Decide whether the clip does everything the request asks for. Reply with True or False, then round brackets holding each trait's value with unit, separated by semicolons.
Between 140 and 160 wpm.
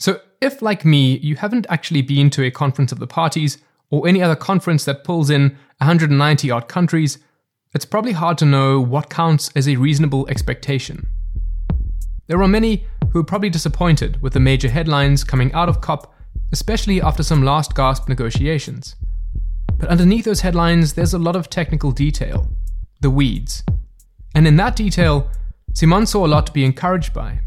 False (175 wpm)